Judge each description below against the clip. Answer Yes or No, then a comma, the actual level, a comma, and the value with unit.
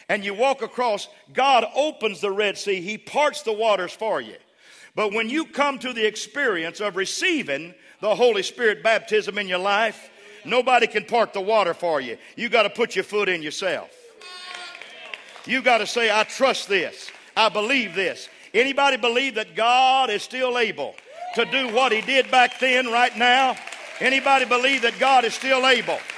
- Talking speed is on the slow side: No, average, 180 wpm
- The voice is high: Yes, high, 240 Hz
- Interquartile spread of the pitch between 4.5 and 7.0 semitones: No, average, 3.8 semitones